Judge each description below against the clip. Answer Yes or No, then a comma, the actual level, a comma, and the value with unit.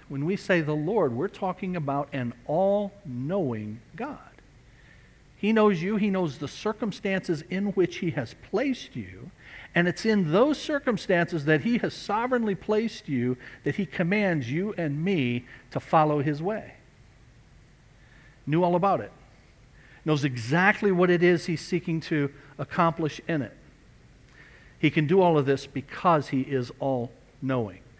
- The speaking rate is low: No, average, 155 wpm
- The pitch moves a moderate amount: No, wide, 6.1 semitones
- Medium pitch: Yes, medium, 165 Hz